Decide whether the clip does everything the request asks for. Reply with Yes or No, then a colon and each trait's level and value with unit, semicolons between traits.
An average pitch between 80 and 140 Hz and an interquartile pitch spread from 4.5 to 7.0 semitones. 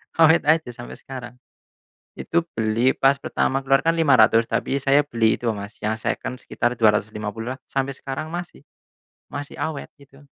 No: low, 135 Hz; average, 3.9 semitones